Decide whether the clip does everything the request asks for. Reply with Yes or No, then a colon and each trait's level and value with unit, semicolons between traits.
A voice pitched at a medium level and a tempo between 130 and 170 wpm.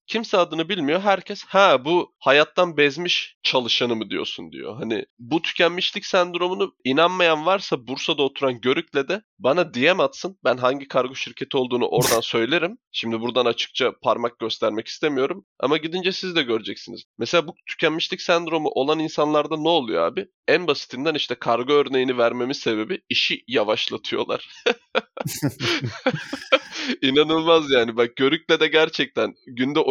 Yes: medium, 160 Hz; average, 135 wpm